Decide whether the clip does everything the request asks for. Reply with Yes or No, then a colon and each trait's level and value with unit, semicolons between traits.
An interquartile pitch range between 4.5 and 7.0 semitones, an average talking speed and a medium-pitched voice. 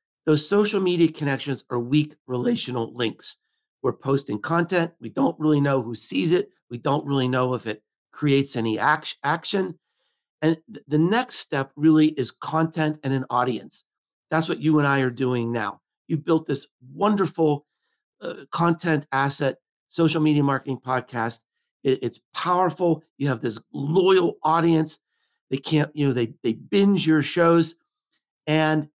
No: average, 4.1 semitones; average, 155 wpm; medium, 150 Hz